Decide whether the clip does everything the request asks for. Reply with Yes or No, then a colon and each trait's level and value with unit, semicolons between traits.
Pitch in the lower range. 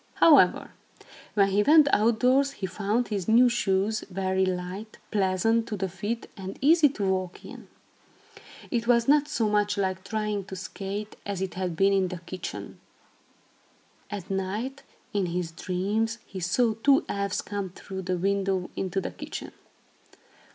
No: high, 200 Hz